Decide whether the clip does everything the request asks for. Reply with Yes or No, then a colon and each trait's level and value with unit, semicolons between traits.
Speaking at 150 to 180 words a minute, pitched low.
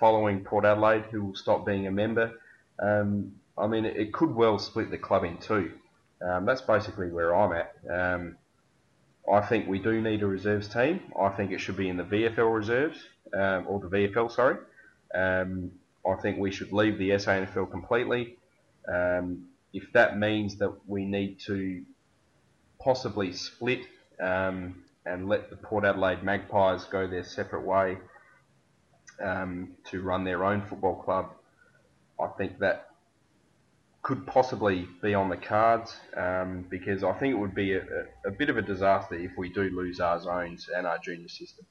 Yes: average, 170 wpm; low, 100 Hz